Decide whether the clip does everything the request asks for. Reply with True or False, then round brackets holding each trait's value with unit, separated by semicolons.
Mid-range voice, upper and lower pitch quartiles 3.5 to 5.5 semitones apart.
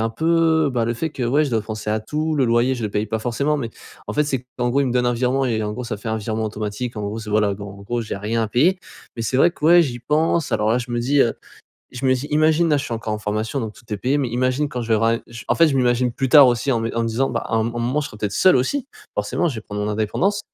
False (120 Hz; 4.1 semitones)